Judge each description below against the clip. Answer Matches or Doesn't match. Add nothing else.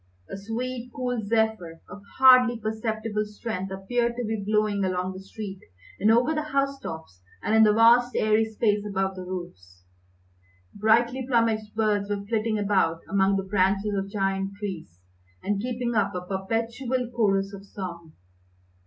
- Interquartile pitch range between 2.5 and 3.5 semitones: Matches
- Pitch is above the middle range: Matches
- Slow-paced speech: Doesn't match